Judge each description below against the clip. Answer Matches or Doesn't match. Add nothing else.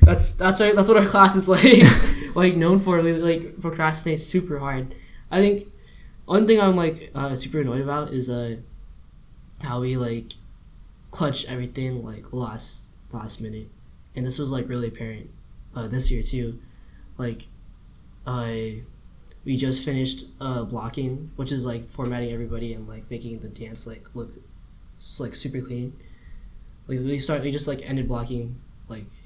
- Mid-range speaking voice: Doesn't match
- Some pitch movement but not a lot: Matches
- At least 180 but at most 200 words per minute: Doesn't match